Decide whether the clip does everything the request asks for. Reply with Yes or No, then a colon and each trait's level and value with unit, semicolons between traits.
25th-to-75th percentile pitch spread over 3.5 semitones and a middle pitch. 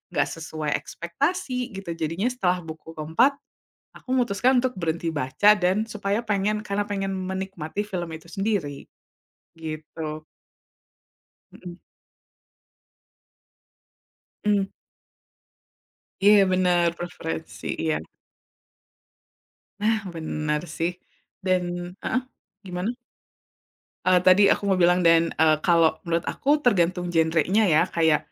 Yes: average, 3.9 semitones; medium, 180 Hz